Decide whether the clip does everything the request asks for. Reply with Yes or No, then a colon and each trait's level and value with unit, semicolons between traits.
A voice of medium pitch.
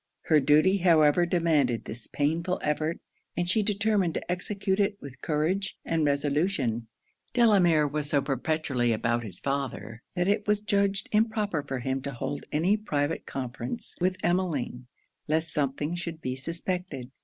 Yes: medium, 160 Hz